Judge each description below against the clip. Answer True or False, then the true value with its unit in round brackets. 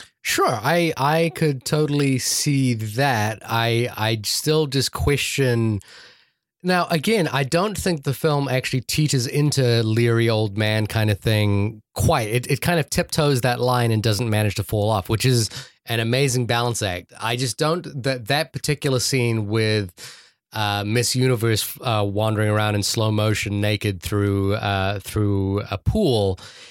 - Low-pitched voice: True (120 Hz)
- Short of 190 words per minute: True (160 wpm)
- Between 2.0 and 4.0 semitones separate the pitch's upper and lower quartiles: False (4.6 semitones)